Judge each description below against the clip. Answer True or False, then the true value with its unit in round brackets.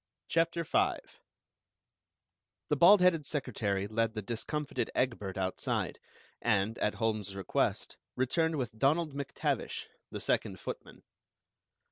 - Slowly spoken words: True (110 wpm)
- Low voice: True (120 Hz)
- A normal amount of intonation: False (6.2 semitones)